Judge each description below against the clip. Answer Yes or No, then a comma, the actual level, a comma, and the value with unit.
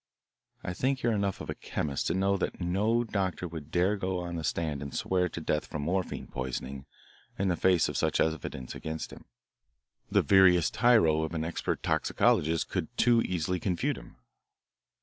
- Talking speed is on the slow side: No, average, 185 wpm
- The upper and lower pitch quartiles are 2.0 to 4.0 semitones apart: Yes, average, 3.5 semitones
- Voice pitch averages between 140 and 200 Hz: No, very low, 90 Hz